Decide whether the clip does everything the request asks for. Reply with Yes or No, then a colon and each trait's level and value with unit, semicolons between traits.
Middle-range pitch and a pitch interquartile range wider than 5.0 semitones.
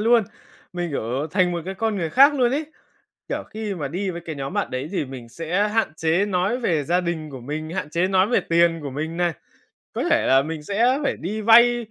Yes: medium, 175 Hz; wide, 5.4 semitones